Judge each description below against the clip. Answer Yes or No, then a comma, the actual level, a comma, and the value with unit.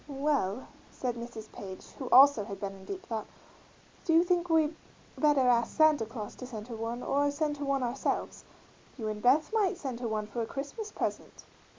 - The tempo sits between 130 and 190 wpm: No, average, 200 wpm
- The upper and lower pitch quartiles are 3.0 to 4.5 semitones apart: No, average, 5.0 semitones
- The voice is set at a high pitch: Yes, very high, 255 Hz